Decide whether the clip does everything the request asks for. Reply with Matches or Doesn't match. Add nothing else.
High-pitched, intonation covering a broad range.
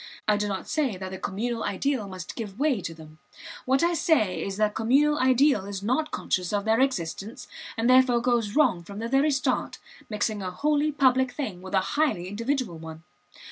Matches